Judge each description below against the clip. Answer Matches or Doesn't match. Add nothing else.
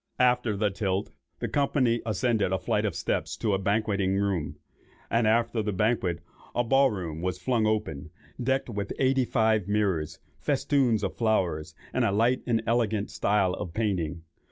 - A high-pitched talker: Doesn't match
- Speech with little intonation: Doesn't match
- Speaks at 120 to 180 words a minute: Matches